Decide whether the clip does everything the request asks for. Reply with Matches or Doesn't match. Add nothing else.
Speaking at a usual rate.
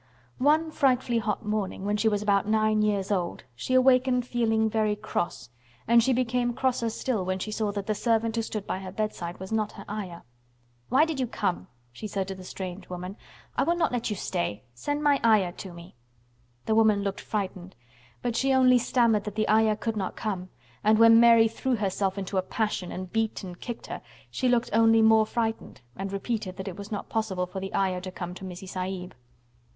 Doesn't match